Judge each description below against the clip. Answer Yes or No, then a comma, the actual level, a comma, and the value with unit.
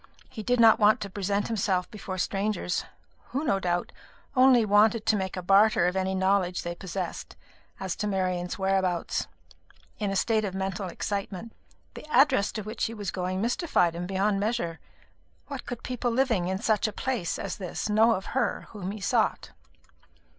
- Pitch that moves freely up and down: No, average, 3.0 semitones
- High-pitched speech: Yes, high, 200 Hz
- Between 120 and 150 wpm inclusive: No, average, 175 wpm